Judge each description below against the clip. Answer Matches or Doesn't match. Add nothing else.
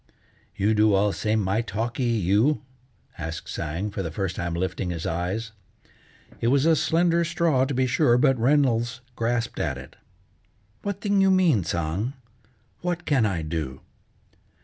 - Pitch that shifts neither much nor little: Doesn't match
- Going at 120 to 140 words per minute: Doesn't match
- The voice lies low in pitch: Matches